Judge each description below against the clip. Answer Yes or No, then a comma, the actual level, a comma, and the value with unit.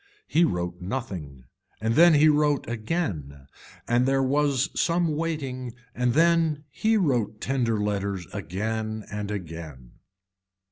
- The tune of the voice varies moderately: No, wide, 7.0 semitones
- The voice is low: Yes, low, 120 Hz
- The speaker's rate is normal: No, slow, 125 wpm